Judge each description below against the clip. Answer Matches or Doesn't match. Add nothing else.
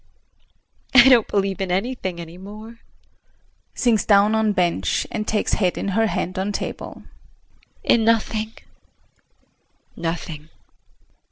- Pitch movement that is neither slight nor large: Matches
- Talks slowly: Matches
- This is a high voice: Matches